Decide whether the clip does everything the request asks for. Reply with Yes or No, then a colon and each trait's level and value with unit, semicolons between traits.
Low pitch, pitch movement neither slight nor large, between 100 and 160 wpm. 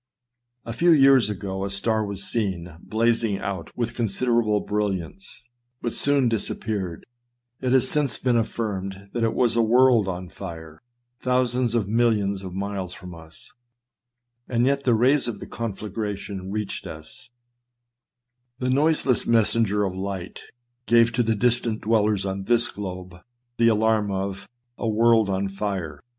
Yes: low, 110 Hz; average, 3.5 semitones; average, 155 wpm